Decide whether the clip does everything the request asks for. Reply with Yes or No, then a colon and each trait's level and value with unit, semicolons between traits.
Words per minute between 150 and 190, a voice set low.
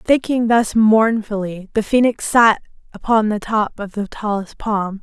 No: average, 155 wpm; high, 215 Hz